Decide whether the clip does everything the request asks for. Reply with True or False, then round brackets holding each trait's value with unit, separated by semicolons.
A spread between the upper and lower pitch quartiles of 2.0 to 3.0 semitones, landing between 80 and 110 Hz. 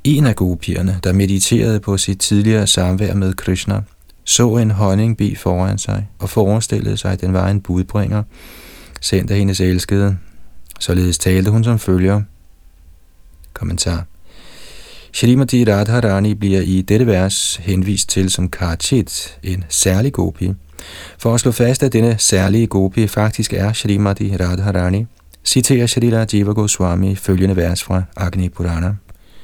True (2.7 semitones; 95 Hz)